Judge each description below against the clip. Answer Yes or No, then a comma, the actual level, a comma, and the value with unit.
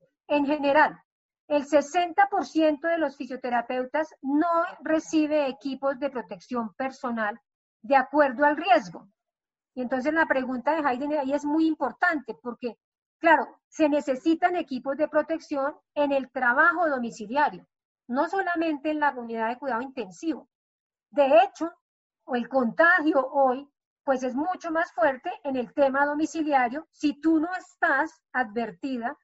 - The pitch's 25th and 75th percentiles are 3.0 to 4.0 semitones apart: Yes, average, 3.5 semitones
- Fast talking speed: No, slow, 135 wpm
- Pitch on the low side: No, very high, 290 Hz